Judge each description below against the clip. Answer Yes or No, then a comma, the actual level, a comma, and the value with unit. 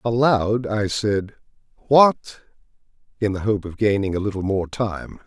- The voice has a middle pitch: No, low, 105 Hz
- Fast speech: No, average, 150 wpm